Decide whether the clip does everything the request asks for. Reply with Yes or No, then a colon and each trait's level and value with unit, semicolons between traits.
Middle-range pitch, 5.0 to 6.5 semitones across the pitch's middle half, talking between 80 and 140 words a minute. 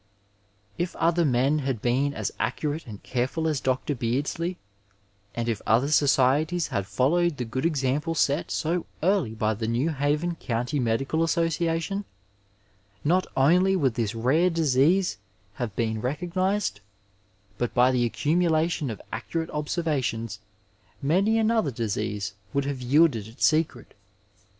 Yes: medium, 145 Hz; wide, 5.5 semitones; slow, 135 wpm